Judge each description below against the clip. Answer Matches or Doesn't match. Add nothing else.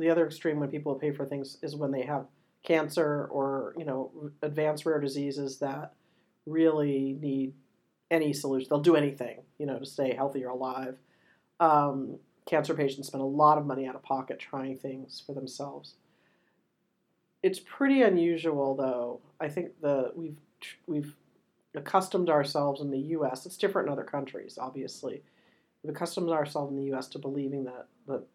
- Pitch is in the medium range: Matches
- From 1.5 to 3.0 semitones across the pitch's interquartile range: Matches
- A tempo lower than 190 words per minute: Matches